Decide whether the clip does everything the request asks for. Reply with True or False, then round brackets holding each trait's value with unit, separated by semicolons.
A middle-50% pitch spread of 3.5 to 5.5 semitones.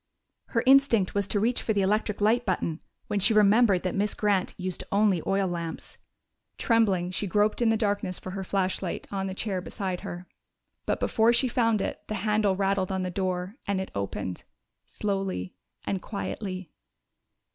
False (2.5 semitones)